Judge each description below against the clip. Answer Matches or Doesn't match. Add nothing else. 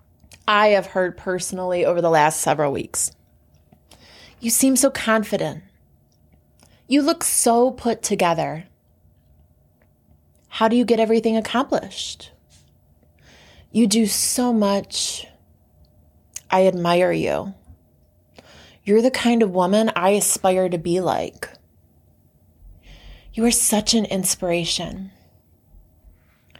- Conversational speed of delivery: Doesn't match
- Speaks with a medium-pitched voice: Matches